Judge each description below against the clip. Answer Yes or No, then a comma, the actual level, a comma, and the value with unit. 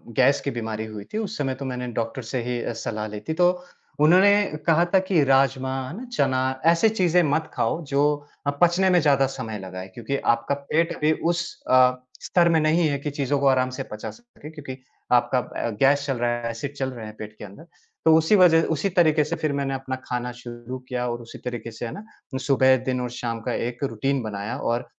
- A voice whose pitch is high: No, low, 135 Hz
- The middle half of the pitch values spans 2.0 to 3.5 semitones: No, average, 4.7 semitones